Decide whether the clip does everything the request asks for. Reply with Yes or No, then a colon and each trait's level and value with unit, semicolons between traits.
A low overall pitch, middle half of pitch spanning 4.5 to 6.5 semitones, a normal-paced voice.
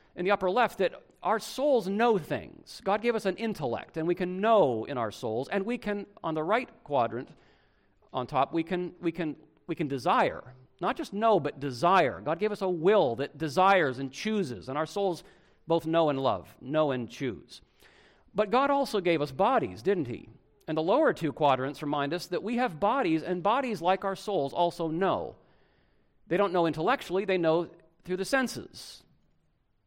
No: medium, 180 Hz; average, 4.8 semitones; average, 195 wpm